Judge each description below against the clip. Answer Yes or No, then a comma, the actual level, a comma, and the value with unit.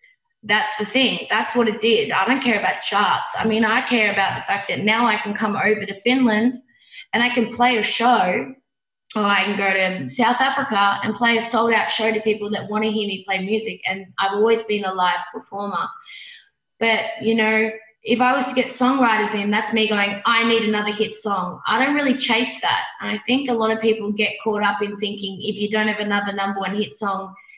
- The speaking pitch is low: No, high, 220 Hz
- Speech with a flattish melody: Yes, narrow, 2.3 semitones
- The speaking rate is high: Yes, fast, 230 wpm